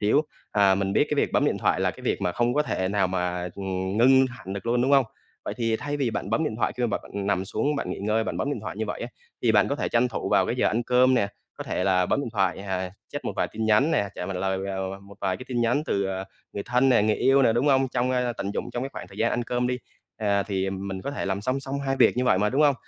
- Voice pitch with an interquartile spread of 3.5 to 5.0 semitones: Yes, average, 4.6 semitones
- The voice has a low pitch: Yes, low, 110 Hz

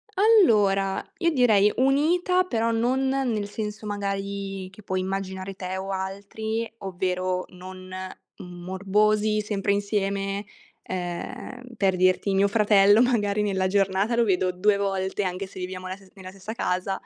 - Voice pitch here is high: Yes, high, 200 Hz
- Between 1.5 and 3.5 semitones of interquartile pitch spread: Yes, narrow, 2.4 semitones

